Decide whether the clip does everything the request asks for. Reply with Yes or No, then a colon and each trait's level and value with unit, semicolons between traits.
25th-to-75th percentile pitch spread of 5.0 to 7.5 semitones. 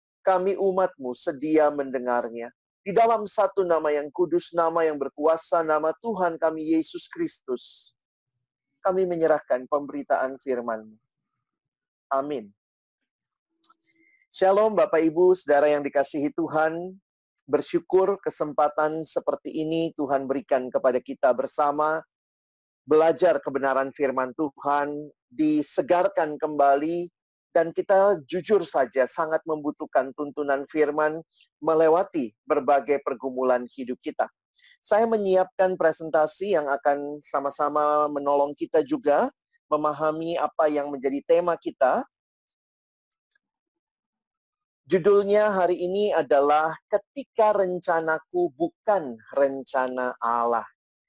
Yes: average, 5.3 semitones